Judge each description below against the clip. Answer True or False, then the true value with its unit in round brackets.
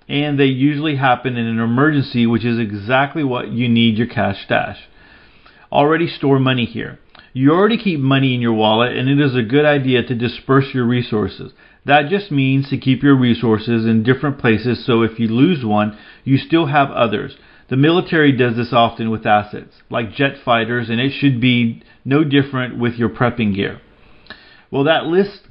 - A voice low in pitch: True (125 Hz)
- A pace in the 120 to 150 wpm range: False (185 wpm)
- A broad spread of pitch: False (3.4 semitones)